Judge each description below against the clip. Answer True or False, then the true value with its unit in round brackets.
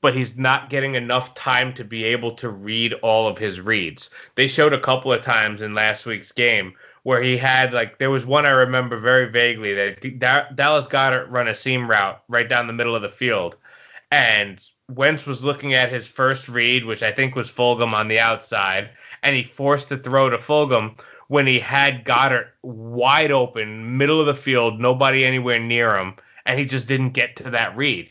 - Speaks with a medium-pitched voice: False (125 Hz)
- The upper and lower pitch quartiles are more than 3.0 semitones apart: False (2.5 semitones)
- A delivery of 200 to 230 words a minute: True (205 wpm)